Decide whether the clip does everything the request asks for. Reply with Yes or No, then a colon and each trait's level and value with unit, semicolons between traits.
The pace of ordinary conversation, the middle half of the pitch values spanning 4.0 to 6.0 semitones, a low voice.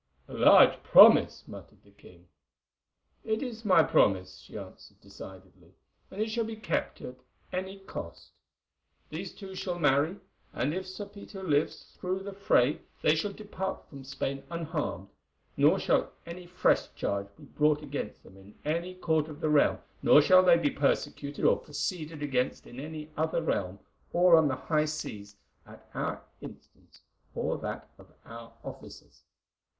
No: average, 160 wpm; wide, 5.5 semitones; medium, 155 Hz